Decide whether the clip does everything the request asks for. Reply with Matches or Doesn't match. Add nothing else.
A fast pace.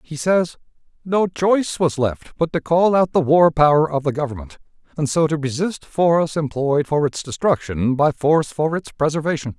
Doesn't match